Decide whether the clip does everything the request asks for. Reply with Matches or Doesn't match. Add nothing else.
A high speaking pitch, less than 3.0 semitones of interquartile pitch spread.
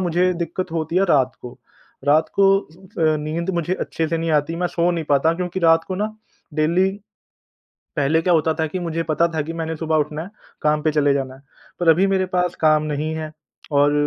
Doesn't match